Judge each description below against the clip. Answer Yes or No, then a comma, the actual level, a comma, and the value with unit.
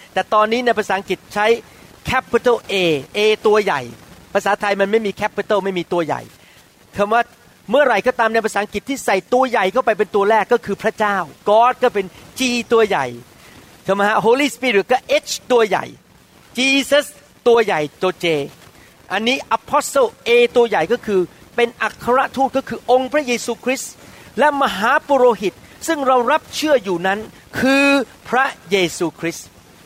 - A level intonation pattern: No, average, 4.6 semitones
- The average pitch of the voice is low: No, high, 225 Hz